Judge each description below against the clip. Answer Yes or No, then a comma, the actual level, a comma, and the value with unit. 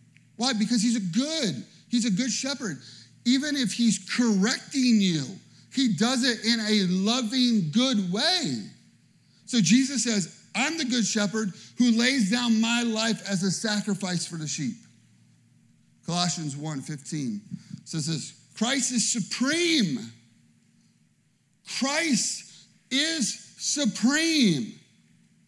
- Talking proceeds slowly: Yes, slow, 120 wpm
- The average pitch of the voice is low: No, high, 220 Hz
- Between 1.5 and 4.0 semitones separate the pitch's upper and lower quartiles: No, average, 4.6 semitones